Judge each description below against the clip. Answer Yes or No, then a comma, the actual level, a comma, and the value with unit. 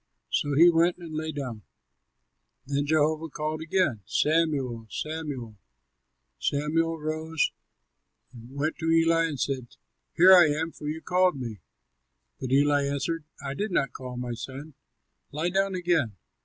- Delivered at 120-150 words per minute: Yes, average, 140 wpm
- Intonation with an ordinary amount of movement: Yes, average, 3.1 semitones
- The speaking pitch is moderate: Yes, medium, 155 Hz